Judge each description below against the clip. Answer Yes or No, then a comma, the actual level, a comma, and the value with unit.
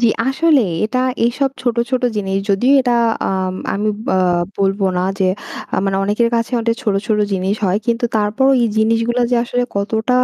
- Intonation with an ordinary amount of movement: Yes, average, 3.8 semitones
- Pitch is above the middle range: Yes, high, 225 Hz